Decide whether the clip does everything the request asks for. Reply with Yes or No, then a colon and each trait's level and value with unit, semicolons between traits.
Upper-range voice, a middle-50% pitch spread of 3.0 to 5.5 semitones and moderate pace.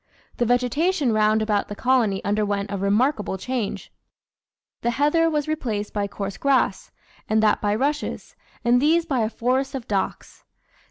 Yes: high, 235 Hz; average, 4.8 semitones; average, 155 wpm